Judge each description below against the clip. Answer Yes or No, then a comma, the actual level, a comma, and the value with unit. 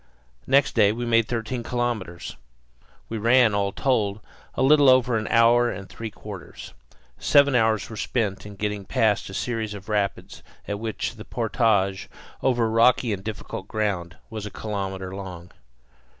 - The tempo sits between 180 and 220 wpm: No, average, 155 wpm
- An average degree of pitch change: Yes, average, 3.0 semitones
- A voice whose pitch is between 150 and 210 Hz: No, low, 110 Hz